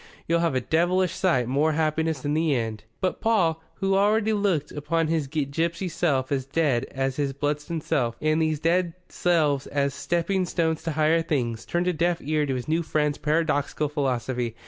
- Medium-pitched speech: Yes, medium, 155 Hz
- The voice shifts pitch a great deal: No, average, 3.2 semitones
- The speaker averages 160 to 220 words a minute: Yes, average, 185 wpm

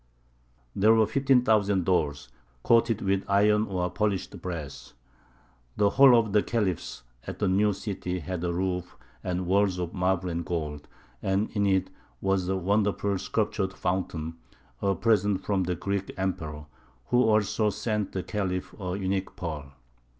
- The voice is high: No, very low, 95 Hz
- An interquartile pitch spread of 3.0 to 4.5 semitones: No, narrow, 2.5 semitones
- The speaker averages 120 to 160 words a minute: Yes, average, 150 wpm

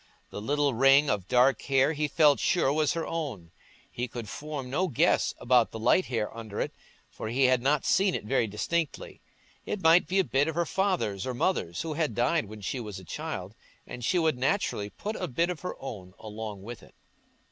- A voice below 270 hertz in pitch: Yes, low, 135 Hz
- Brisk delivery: Yes, fast, 210 wpm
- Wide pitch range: Yes, wide, 6.3 semitones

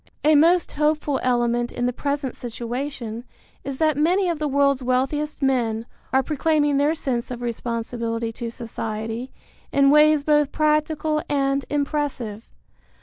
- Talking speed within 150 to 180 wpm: No, average, 140 wpm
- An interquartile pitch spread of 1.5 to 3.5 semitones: No, average, 4.0 semitones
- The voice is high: Yes, very high, 275 Hz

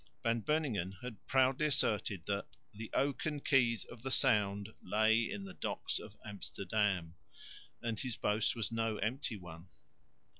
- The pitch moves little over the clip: No, average, 3.7 semitones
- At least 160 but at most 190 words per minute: No, average, 145 wpm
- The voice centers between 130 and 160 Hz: No, low, 110 Hz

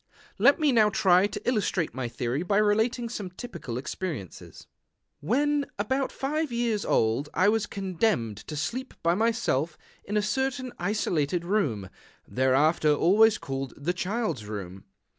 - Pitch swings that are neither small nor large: No, wide, 7.8 semitones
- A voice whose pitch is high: Yes, high, 195 Hz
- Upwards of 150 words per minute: No, average, 145 wpm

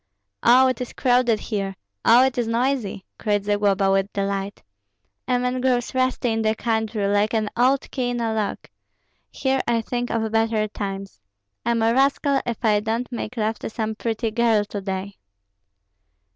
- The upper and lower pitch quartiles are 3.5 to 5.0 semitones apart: No, average, 3.0 semitones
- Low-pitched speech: No, high, 225 Hz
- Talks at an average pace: Yes, average, 170 wpm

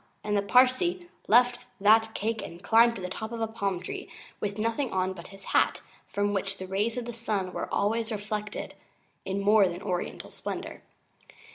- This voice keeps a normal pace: Yes, average, 185 wpm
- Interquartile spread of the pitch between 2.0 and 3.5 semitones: Yes, average, 2.8 semitones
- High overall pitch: Yes, high, 210 Hz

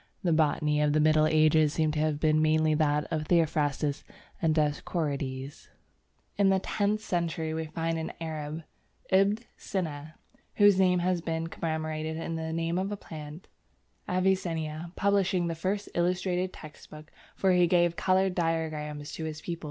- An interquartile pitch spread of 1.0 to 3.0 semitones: Yes, narrow, 2.6 semitones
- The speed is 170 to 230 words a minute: No, average, 160 wpm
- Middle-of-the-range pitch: Yes, medium, 160 Hz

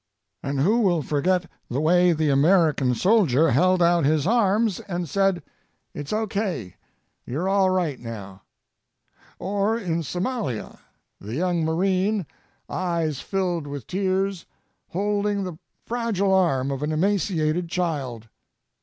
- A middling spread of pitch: Yes, average, 4.6 semitones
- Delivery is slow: Yes, slow, 125 wpm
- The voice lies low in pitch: No, medium, 175 Hz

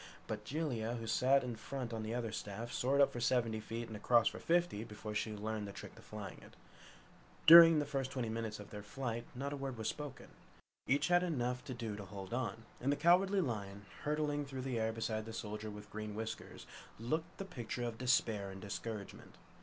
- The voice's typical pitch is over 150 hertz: No, low, 115 Hz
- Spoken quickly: Yes, fast, 210 wpm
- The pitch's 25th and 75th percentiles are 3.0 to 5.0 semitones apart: Yes, average, 4.0 semitones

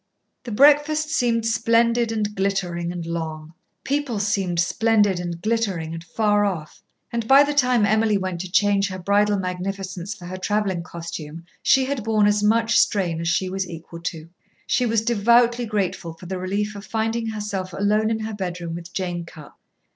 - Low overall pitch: No, high, 200 Hz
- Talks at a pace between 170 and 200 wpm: Yes, average, 175 wpm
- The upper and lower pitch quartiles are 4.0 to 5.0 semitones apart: Yes, average, 4.3 semitones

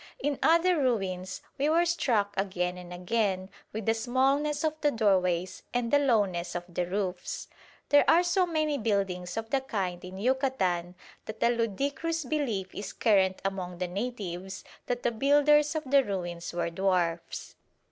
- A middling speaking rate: Yes, average, 160 wpm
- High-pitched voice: Yes, high, 215 Hz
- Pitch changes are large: Yes, wide, 7.1 semitones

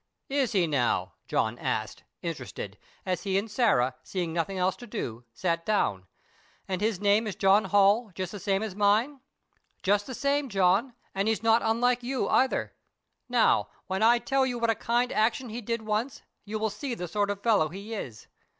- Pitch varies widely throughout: No, average, 3.6 semitones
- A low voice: No, high, 210 Hz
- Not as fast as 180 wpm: No, average, 190 wpm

